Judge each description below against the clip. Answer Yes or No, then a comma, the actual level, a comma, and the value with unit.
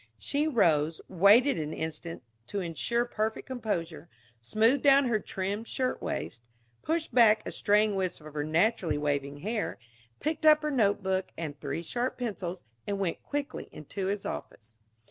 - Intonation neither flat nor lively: No, wide, 6.5 semitones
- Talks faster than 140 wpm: Yes, average, 150 wpm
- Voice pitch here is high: Yes, high, 200 Hz